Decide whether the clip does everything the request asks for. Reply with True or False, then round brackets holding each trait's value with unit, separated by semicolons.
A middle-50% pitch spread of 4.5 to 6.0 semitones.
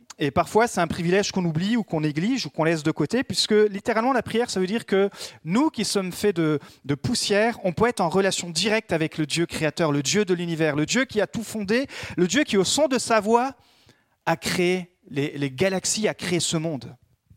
True (5.0 semitones)